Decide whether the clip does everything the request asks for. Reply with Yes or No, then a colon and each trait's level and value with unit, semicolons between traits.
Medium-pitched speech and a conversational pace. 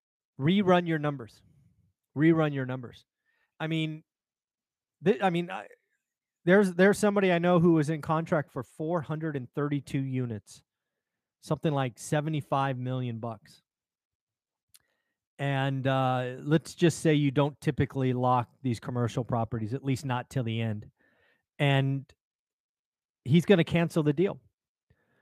No: medium, 145 Hz; slow, 130 wpm